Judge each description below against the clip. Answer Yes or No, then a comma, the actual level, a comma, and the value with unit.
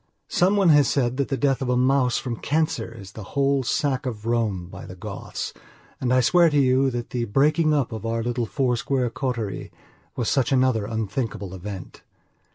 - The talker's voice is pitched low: Yes, low, 125 Hz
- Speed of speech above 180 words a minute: Yes, average, 195 wpm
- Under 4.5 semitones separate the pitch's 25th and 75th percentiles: Yes, average, 3.3 semitones